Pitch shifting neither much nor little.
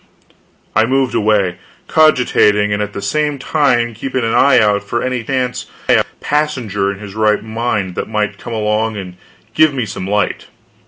Yes: average, 3.8 semitones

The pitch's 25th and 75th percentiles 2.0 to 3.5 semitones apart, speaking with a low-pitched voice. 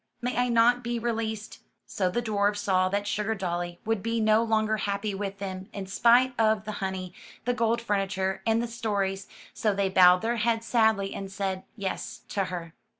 No: average, 2.8 semitones; high, 205 Hz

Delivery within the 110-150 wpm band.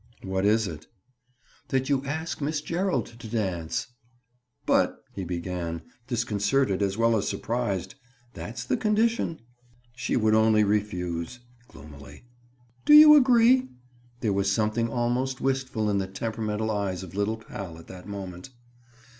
Yes: average, 140 wpm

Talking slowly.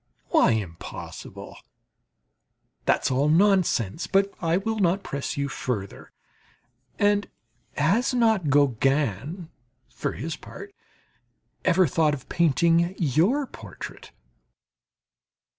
Yes: slow, 95 wpm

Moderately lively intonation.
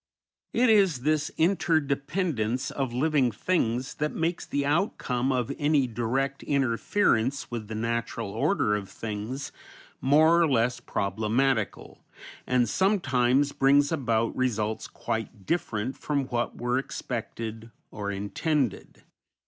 Yes: average, 4.7 semitones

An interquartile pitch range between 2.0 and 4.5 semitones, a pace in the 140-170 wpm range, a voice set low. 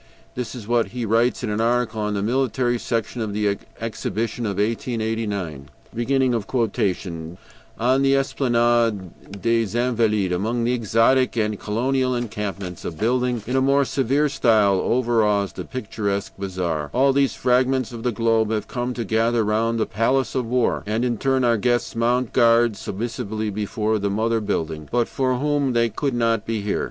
Yes: average, 2.8 semitones; average, 165 wpm; low, 115 Hz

